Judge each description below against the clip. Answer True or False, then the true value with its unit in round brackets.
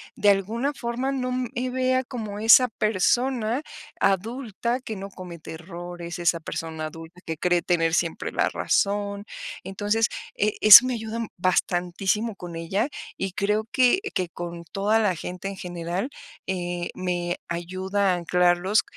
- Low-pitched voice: False (195 Hz)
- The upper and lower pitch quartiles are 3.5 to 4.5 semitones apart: True (4.2 semitones)